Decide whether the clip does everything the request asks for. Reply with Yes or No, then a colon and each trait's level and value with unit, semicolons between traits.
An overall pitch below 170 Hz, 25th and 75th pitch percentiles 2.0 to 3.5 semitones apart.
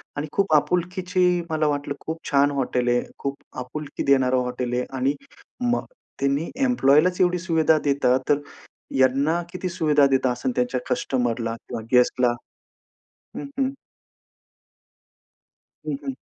No: medium, 140 Hz; average, 4.5 semitones